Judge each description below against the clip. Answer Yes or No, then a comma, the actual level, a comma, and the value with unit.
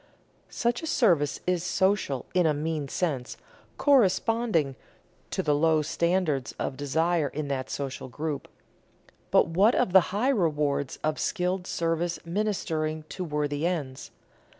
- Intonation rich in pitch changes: No, average, 4.2 semitones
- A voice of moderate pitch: Yes, medium, 165 Hz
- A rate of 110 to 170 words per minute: Yes, slow, 135 wpm